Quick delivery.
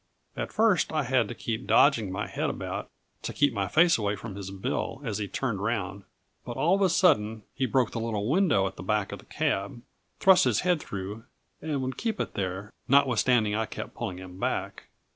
Yes: fast, 210 wpm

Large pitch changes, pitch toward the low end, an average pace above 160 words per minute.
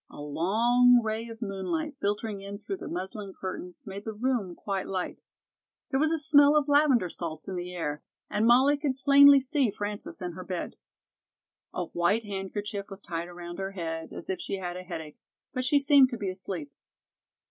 No: wide, 6.2 semitones; high, 205 Hz; average, 190 wpm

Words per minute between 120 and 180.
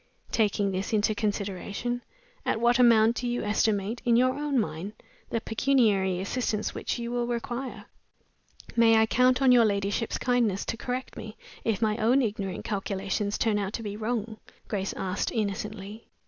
Yes: average, 160 wpm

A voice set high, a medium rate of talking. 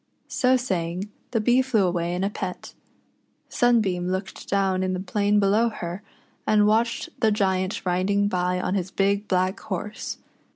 Yes: high, 195 Hz; average, 160 wpm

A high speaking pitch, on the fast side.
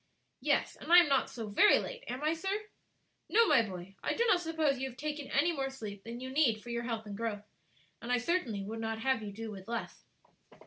Yes: high, 245 Hz; fast, 235 wpm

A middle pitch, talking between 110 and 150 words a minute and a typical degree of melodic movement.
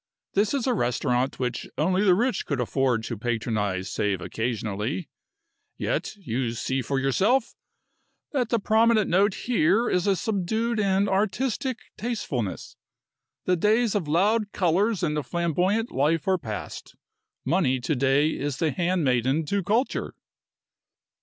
No: medium, 175 Hz; average, 140 wpm; wide, 8.2 semitones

